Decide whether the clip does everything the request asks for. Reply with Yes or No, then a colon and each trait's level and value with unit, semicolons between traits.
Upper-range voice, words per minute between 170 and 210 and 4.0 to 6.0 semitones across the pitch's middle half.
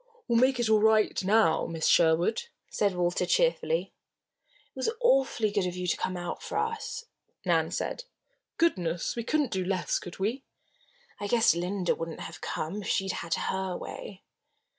Yes: high, 200 Hz; average, 175 wpm; average, 5.2 semitones